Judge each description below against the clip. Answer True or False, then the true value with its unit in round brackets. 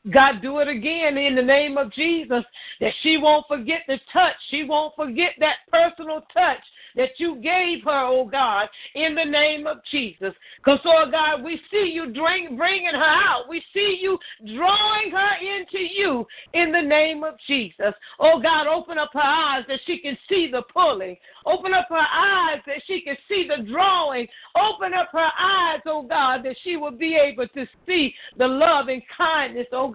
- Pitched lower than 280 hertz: False (310 Hz)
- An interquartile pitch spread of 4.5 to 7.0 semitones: False (3.8 semitones)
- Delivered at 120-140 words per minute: False (190 wpm)